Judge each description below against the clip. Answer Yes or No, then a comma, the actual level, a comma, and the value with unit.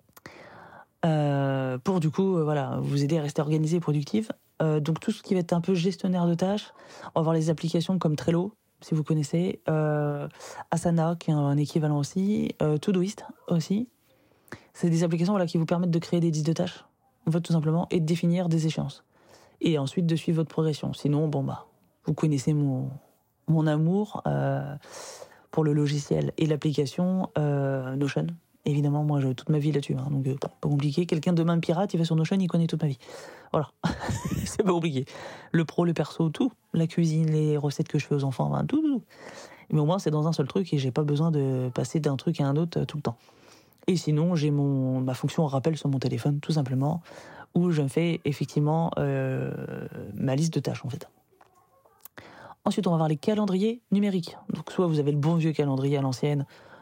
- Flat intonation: No, average, 3.1 semitones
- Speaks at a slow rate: No, average, 210 wpm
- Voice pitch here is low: No, medium, 160 Hz